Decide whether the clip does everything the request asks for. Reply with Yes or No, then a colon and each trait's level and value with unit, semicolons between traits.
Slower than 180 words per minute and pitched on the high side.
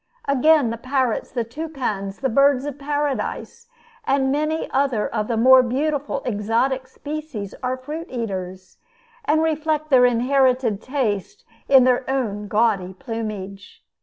Yes: slow, 135 wpm; very high, 255 Hz